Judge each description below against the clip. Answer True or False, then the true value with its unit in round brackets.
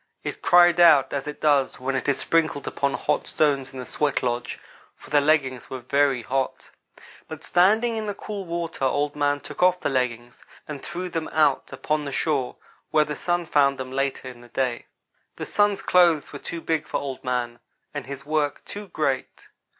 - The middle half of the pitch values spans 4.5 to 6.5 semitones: False (3.7 semitones)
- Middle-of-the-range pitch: True (145 Hz)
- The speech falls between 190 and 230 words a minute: True (195 wpm)